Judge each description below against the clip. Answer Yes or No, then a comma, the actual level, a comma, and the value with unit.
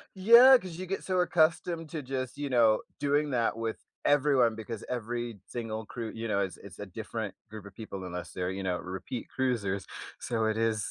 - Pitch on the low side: Yes, low, 115 Hz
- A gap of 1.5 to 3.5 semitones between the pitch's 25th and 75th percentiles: No, wide, 5.4 semitones